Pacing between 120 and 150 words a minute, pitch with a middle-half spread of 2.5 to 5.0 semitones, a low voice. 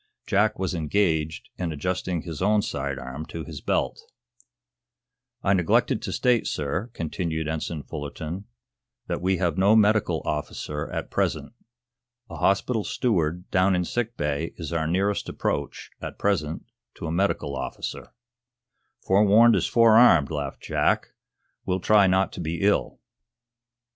Yes: average, 140 wpm; average, 4.3 semitones; very low, 90 Hz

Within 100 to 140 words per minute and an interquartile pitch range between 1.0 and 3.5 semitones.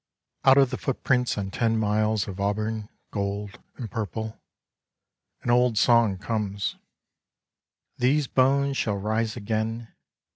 Yes: slow, 135 wpm; average, 3.0 semitones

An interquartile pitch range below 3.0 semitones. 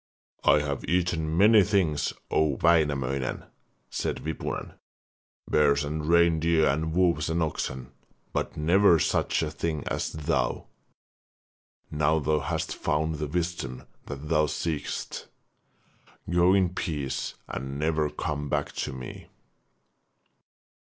Yes: narrow, 2.6 semitones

